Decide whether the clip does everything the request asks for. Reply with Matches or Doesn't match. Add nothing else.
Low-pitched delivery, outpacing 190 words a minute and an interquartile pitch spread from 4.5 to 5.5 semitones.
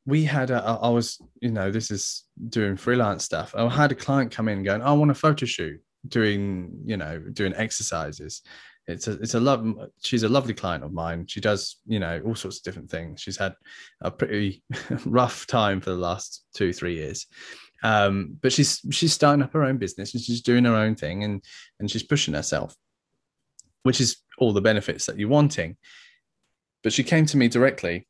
Matches